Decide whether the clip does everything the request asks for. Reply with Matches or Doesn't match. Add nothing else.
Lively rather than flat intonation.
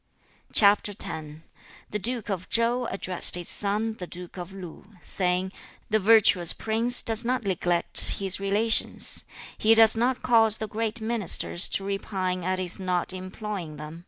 Doesn't match